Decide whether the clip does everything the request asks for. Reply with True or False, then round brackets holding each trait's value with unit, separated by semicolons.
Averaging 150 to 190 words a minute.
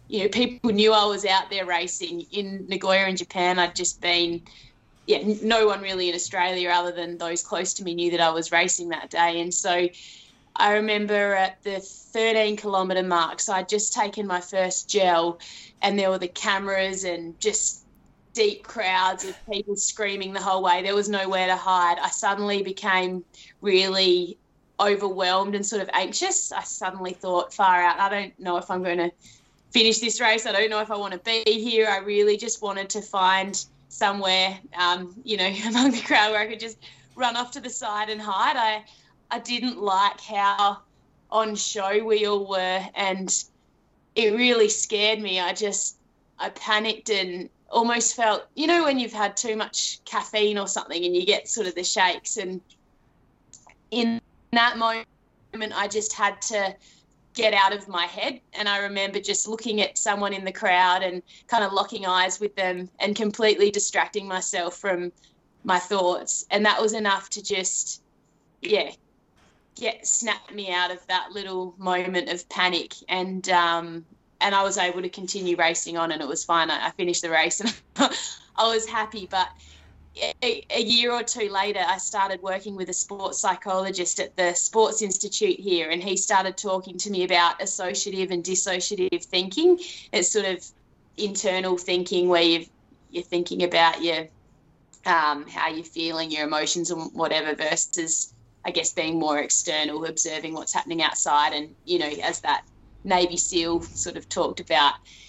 True (180 wpm)